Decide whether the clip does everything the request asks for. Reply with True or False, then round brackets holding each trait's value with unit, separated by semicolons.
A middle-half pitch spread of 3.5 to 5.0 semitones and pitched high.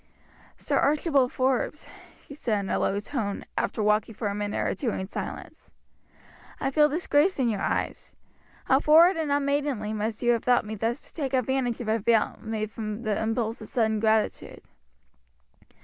True (4.4 semitones; 235 Hz)